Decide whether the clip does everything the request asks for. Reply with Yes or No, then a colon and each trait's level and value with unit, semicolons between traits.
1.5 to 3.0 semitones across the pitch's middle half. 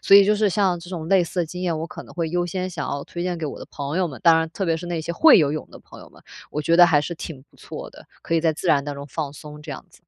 Yes: average, 2.7 semitones